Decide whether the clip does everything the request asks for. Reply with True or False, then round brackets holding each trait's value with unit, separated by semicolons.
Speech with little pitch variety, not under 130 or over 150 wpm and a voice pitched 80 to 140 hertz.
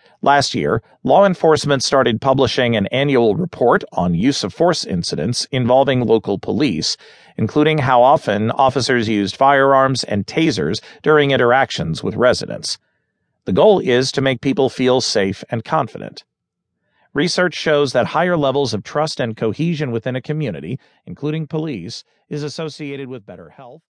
False (3.6 semitones; 145 wpm; 135 Hz)